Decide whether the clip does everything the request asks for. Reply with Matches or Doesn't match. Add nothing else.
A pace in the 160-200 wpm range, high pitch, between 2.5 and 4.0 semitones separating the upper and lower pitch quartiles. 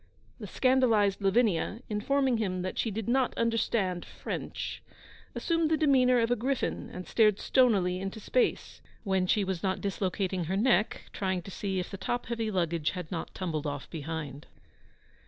Doesn't match